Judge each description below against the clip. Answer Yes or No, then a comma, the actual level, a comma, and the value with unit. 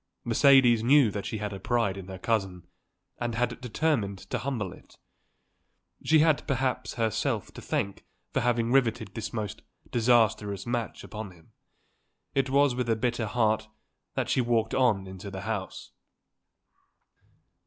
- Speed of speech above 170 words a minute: No, average, 150 wpm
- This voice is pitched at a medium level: No, low, 115 Hz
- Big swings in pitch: No, average, 3.4 semitones